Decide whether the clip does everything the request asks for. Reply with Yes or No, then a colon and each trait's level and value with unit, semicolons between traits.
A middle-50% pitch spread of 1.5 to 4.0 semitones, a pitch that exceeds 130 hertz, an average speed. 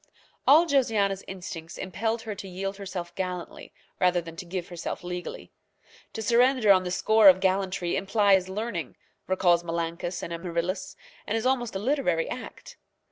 Yes: average, 3.7 semitones; high, 190 Hz; average, 155 wpm